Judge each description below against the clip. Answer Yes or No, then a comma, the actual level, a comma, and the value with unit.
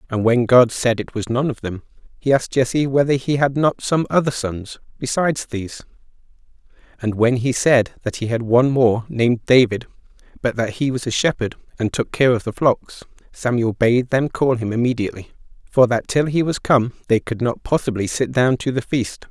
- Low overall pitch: Yes, low, 125 Hz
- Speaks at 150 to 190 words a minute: No, average, 200 wpm